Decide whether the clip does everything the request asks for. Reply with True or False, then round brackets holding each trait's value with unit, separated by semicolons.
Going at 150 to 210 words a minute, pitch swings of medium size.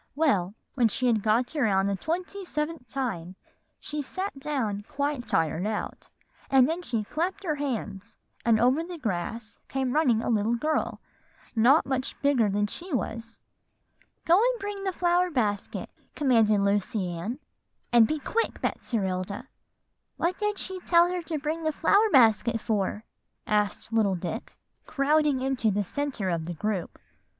False (155 wpm; 6.9 semitones)